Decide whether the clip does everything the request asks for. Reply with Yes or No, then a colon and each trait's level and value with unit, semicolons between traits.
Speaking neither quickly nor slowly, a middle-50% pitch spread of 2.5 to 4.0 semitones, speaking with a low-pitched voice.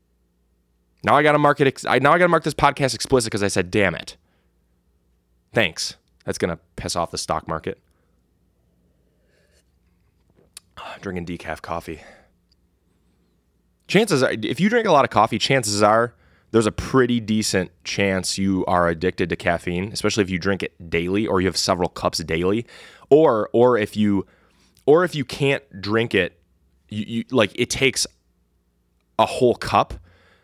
No: average, 160 wpm; average, 4.8 semitones; very low, 90 Hz